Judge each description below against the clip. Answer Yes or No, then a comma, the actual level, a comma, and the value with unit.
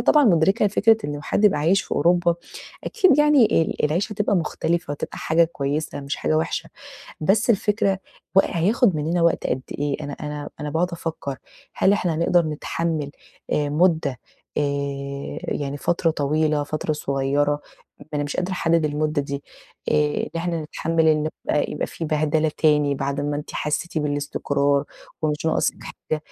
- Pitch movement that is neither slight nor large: Yes, average, 3.0 semitones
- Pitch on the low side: No, medium, 155 Hz